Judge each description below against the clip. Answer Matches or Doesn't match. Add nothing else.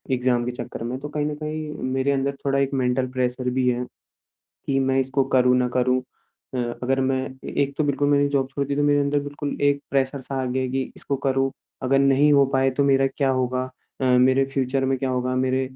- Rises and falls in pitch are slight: Matches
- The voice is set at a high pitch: Doesn't match